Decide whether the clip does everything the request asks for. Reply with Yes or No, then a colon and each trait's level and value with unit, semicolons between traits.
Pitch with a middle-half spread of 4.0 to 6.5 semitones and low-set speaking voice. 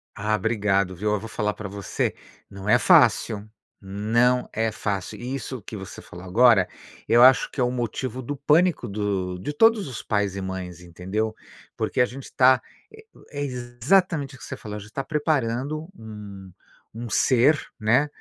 Yes: average, 4.4 semitones; low, 115 Hz